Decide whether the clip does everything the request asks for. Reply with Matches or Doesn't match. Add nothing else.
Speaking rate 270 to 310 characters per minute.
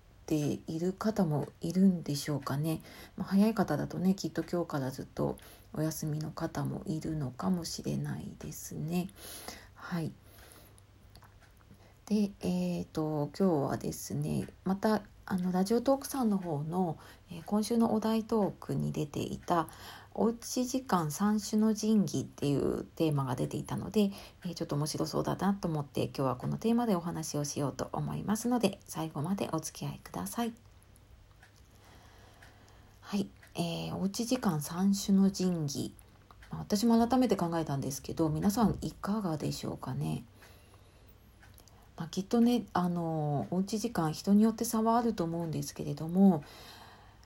Matches